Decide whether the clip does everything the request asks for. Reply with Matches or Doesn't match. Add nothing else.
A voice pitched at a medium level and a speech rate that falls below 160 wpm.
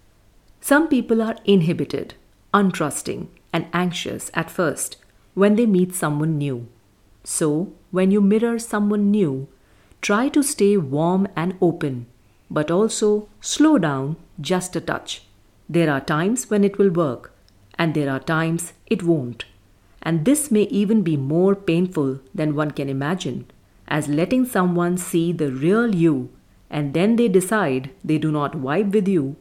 Matches